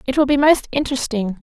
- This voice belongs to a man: No, female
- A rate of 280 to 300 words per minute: No, fast, 205 wpm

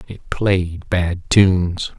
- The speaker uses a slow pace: Yes, slow, 120 wpm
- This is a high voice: No, very low, 90 Hz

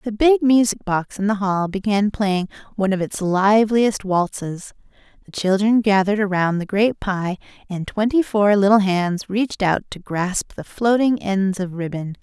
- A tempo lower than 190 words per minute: Yes, average, 170 wpm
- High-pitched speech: Yes, high, 200 Hz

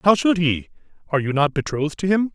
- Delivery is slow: No, fast, 230 wpm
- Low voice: No, medium, 165 Hz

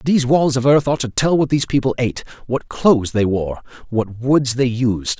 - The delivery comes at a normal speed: No, fast, 220 wpm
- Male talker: Yes, male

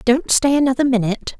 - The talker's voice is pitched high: Yes, very high, 255 Hz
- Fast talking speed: No, average, 175 wpm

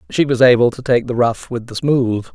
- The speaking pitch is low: Yes, low, 120 Hz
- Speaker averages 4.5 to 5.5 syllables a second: Yes, 5.2 syllables/s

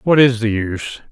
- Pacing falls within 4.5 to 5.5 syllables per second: Yes, 5.3 syllables/s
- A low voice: Yes, low, 115 Hz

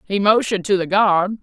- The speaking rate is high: Yes, fast, 210 wpm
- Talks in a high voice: Yes, high, 200 Hz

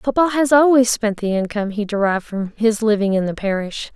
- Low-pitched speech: No, high, 220 Hz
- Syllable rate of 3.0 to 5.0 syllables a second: No, 5.6 syllables/s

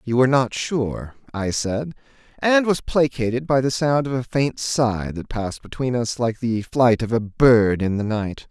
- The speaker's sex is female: No, male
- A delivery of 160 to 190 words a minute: No, fast, 205 wpm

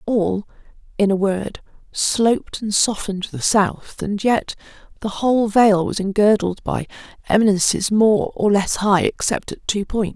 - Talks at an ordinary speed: Yes, average, 160 wpm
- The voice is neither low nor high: No, high, 205 Hz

